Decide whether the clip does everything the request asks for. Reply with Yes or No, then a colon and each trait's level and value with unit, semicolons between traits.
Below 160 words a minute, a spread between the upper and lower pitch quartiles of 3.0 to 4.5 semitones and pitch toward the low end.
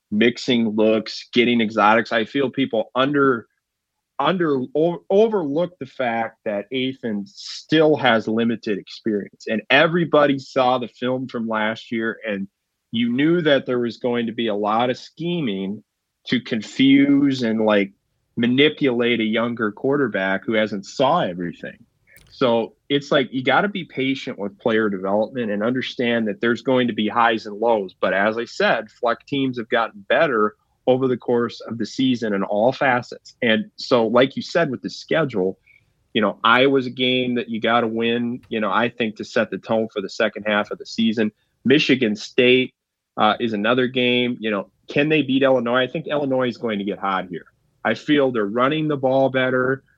No: average, 180 wpm; average, 3.4 semitones; low, 120 Hz